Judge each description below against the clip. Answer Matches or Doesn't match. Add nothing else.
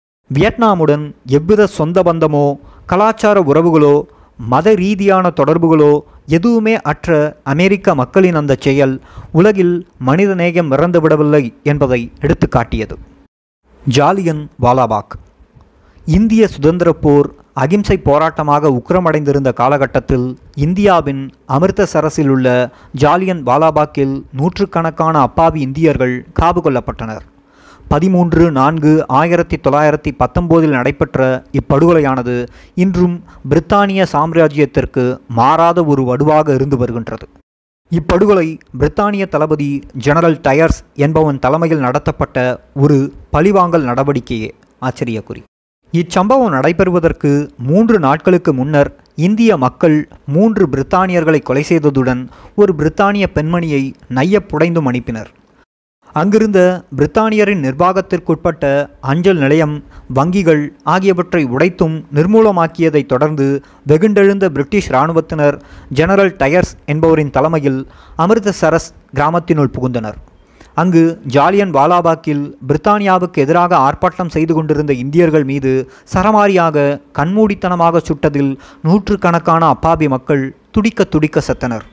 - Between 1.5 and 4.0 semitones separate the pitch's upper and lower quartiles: Doesn't match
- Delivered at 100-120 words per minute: Doesn't match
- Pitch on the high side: Doesn't match